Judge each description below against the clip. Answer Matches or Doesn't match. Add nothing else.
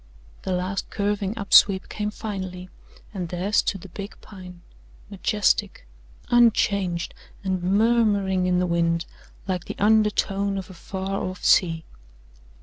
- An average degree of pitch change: Doesn't match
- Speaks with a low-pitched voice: Doesn't match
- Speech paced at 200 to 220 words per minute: Doesn't match